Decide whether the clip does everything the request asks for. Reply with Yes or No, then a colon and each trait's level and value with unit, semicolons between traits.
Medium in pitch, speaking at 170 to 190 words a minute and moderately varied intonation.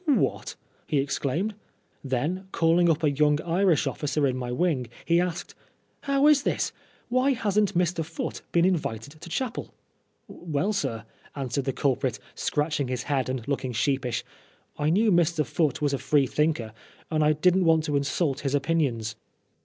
Yes: medium, 150 Hz; average, 180 wpm; average, 4.3 semitones